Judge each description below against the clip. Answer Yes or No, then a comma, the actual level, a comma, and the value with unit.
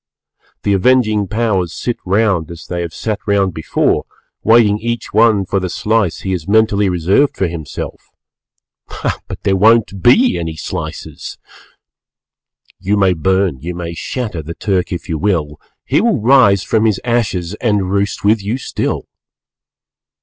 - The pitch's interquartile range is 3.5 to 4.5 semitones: Yes, average, 3.9 semitones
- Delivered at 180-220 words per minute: No, average, 150 wpm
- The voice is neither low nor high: No, low, 100 Hz